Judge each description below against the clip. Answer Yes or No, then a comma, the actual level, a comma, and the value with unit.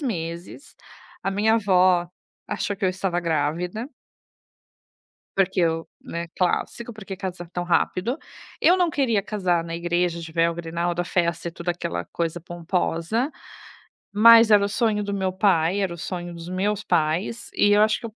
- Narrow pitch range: No, average, 3.3 semitones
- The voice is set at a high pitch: No, medium, 180 Hz